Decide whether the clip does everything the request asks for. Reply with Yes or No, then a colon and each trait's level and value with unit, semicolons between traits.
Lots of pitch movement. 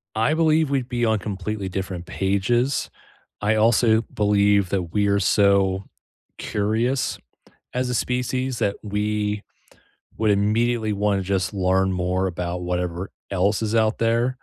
No: average, 3.2 semitones